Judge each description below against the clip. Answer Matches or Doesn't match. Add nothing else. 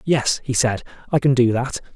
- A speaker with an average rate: Doesn't match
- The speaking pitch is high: Doesn't match